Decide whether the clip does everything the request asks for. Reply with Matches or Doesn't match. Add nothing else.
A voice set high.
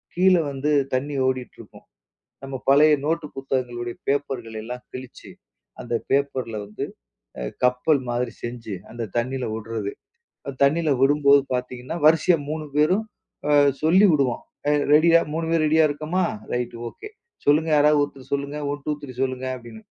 Doesn't match